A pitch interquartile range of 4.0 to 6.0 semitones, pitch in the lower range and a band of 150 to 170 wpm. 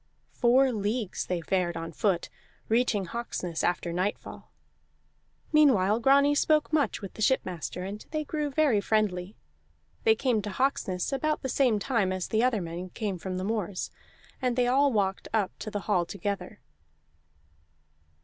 No: wide, 5.6 semitones; high, 210 Hz; average, 155 wpm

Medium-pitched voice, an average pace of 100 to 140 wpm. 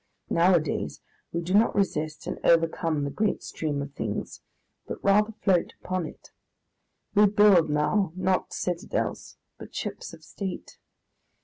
Yes: medium, 175 Hz; slow, 135 wpm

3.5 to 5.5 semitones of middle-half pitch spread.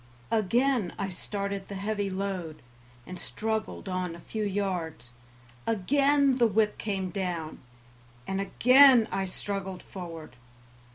No: average, 3.1 semitones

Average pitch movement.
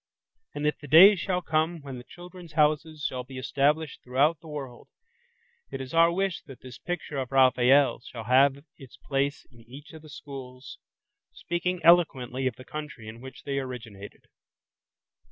Yes: average, 3.7 semitones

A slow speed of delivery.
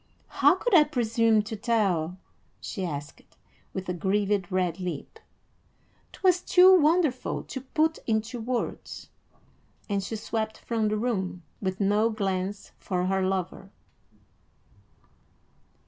Yes: slow, 120 wpm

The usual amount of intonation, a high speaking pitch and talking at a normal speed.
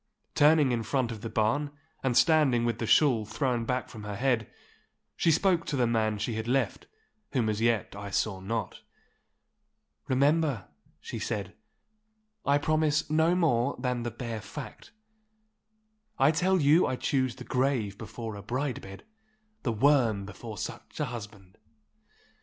No: average, 4.6 semitones; low, 120 Hz; average, 155 wpm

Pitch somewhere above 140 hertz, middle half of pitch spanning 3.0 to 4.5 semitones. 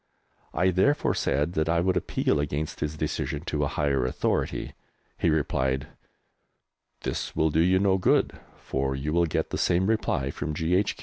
No: very low, 80 Hz; average, 3.9 semitones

